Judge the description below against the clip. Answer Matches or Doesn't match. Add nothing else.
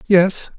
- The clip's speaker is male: Matches